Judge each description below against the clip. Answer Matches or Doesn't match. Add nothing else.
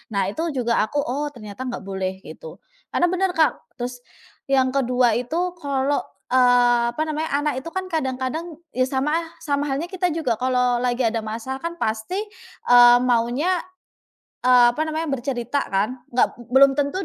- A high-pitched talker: Matches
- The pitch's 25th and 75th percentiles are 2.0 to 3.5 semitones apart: Doesn't match